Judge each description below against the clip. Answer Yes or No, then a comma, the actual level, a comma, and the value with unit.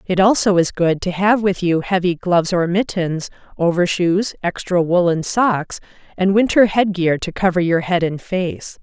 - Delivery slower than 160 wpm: No, average, 170 wpm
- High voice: No, medium, 180 Hz